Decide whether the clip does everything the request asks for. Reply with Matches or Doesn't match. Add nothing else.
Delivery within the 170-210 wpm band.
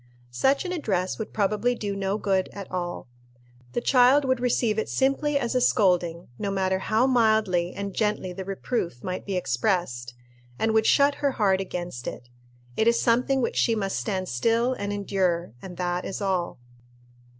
Matches